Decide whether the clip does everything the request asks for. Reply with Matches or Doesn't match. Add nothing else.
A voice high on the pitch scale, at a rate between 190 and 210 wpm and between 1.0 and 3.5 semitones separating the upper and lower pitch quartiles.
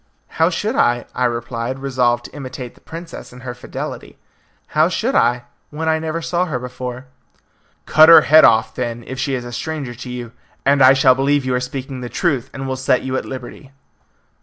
Doesn't match